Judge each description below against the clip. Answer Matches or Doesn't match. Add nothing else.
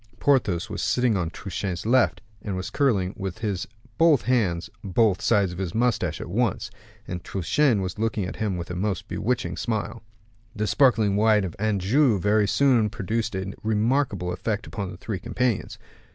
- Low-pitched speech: Matches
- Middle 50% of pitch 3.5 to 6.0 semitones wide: Matches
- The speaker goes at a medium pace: Matches